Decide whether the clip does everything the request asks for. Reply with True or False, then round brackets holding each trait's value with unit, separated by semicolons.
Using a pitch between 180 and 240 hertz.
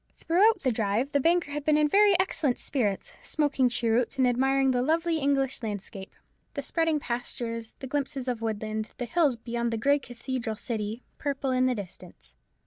False (255 Hz)